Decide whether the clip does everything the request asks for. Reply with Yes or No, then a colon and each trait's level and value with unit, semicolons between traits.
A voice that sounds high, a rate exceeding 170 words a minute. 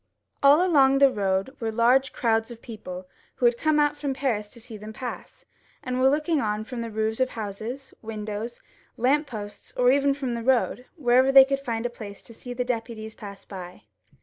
Yes: high, 240 Hz; average, 195 wpm